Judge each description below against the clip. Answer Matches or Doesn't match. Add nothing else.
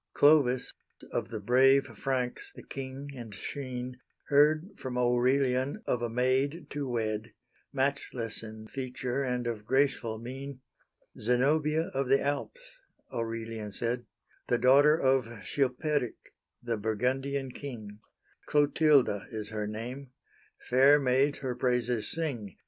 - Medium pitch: Doesn't match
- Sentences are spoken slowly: Matches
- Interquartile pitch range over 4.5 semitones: Doesn't match